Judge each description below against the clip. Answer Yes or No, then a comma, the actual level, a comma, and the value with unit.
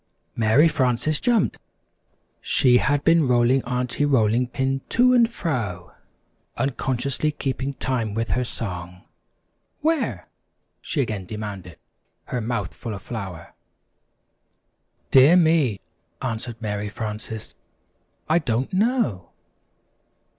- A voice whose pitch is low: Yes, low, 125 Hz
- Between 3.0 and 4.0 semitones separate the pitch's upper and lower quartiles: No, average, 5.1 semitones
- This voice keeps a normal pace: No, slow, 105 wpm